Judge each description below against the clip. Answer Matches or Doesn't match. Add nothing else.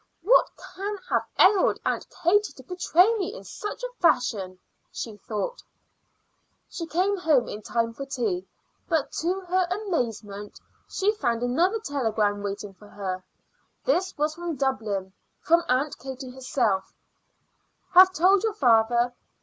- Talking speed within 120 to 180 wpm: Matches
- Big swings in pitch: Matches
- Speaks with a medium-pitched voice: Doesn't match